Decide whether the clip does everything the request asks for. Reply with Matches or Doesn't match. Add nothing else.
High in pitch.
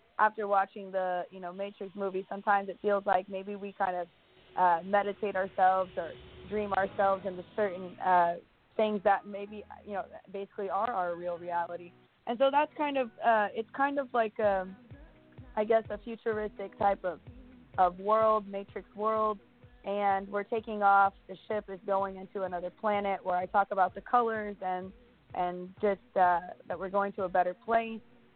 Matches